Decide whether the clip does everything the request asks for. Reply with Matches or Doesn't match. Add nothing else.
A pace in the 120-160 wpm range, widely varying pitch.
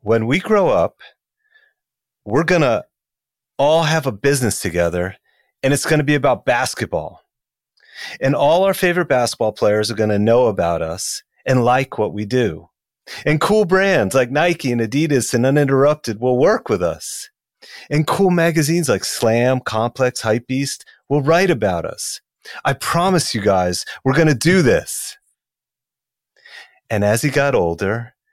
Matches